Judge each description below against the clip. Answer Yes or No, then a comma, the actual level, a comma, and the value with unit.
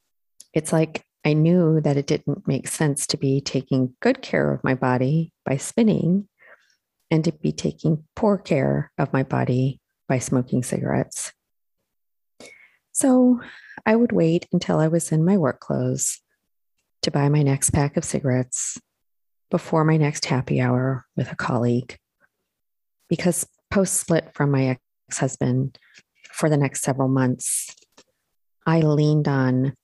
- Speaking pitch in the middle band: Yes, medium, 145 Hz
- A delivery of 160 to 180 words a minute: No, average, 145 wpm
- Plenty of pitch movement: No, average, 4.2 semitones